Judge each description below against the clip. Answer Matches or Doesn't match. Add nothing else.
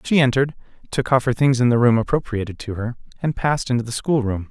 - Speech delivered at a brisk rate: Matches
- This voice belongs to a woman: Doesn't match